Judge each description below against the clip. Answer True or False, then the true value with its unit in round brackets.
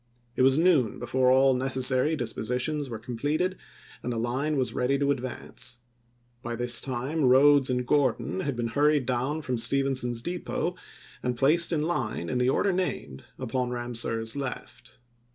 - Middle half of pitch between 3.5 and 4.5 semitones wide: False (3.0 semitones)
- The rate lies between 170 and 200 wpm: False (155 wpm)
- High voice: False (130 Hz)